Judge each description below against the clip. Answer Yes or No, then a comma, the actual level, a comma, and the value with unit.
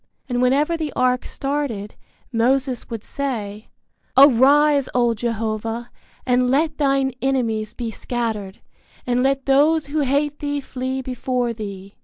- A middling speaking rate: No, slow, 130 wpm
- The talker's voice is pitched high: Yes, very high, 255 Hz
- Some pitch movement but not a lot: Yes, average, 3.3 semitones